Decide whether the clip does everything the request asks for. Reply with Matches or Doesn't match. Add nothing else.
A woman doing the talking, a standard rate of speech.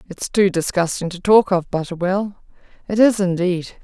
Matches